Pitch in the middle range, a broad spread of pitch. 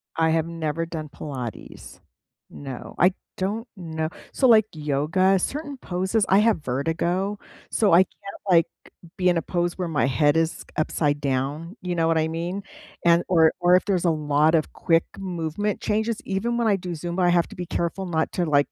No: medium, 170 Hz; average, 3.2 semitones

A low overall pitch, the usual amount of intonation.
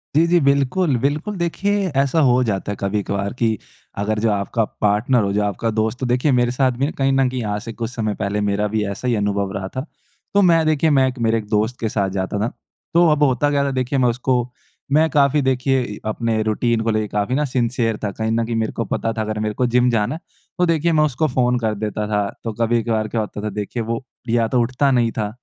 Yes: low, 115 Hz; average, 3.8 semitones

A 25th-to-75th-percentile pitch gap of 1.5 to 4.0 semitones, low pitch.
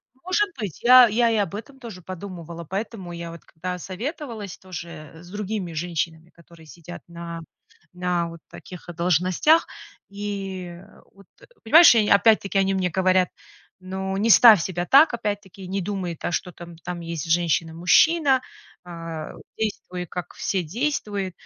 No: average, 3.6 semitones; medium, 185 Hz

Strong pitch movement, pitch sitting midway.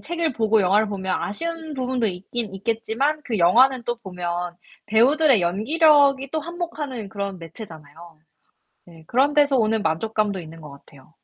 No: wide, 7.3 semitones; high, 220 Hz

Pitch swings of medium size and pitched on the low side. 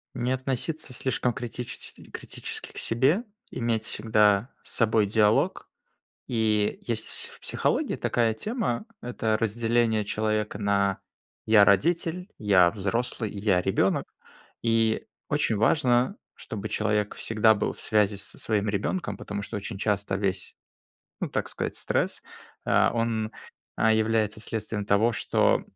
No: narrow, 2.3 semitones; low, 110 Hz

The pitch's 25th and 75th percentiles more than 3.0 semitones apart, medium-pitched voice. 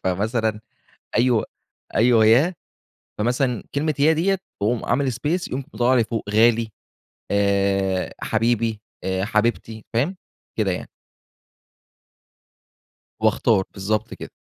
No: average, 3.4 semitones; low, 115 Hz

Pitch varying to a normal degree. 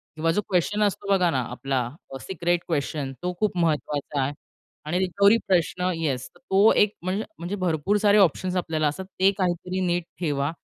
Yes: average, 3.7 semitones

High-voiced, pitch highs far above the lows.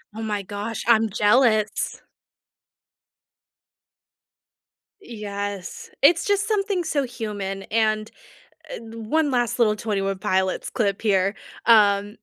No: high, 215 Hz; average, 2.9 semitones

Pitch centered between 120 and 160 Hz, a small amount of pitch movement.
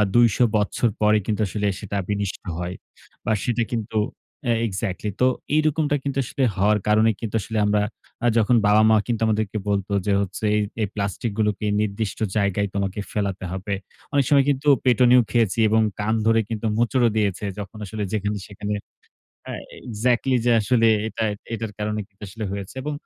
No: low, 105 Hz; narrow, 2.3 semitones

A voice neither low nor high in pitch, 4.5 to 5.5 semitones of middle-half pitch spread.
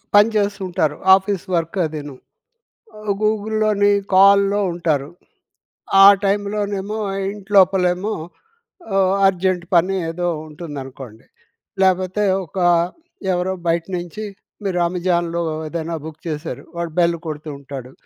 No: medium, 180 Hz; average, 3.4 semitones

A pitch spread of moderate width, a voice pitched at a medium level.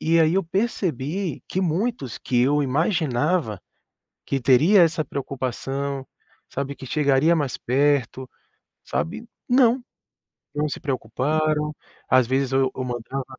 Yes: average, 4.0 semitones; medium, 145 Hz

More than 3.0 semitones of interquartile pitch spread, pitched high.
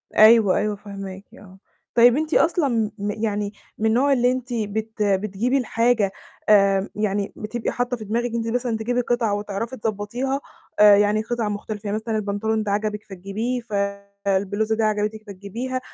No: average, 2.7 semitones; high, 215 Hz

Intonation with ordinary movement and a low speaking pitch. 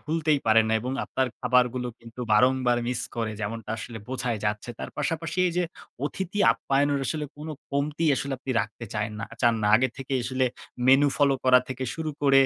Yes: average, 3.5 semitones; low, 130 Hz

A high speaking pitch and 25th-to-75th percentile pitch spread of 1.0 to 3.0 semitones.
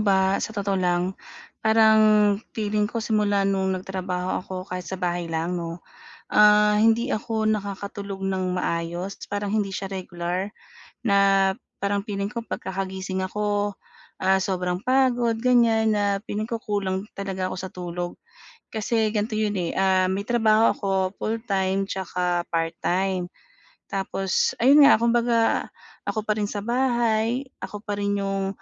Yes: high, 200 Hz; narrow, 2.6 semitones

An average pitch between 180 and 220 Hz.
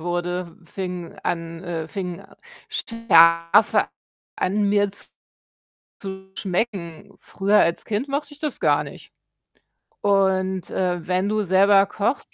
Yes: high, 190 Hz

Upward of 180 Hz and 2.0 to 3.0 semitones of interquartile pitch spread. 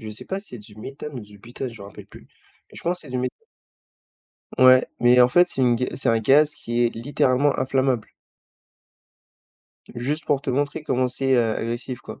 No: low, 125 Hz; average, 2.7 semitones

